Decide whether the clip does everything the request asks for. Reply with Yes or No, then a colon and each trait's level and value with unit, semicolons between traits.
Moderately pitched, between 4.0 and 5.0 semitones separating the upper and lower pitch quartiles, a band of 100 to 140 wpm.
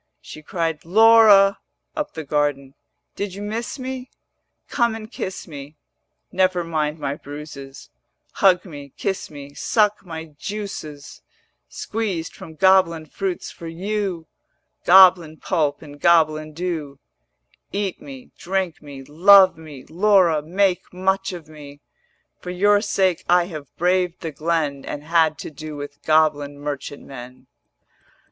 Yes: medium, 165 Hz; average, 4.4 semitones; slow, 135 wpm